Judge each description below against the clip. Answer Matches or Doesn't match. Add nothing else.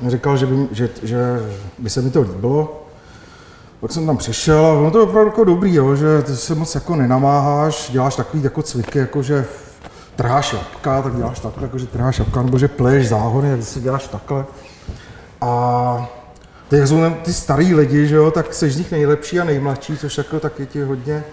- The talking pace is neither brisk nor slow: Doesn't match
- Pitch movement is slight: Doesn't match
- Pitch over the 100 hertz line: Matches